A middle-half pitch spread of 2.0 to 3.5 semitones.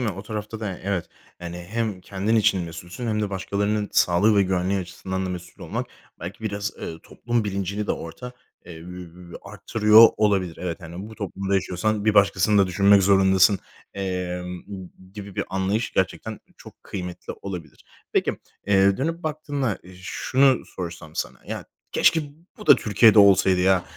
Yes: average, 2.8 semitones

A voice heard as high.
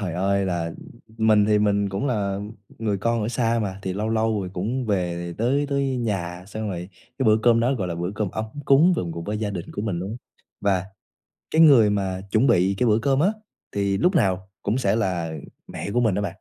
No: low, 105 Hz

